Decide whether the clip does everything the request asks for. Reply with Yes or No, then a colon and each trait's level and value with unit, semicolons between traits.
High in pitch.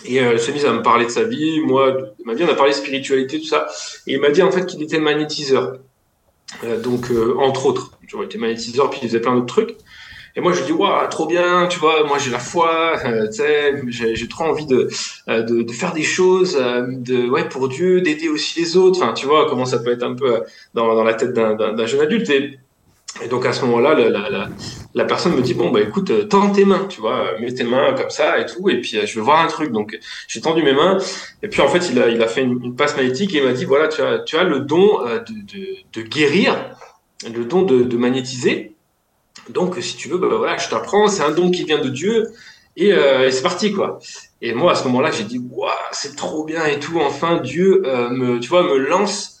No: medium, 155 Hz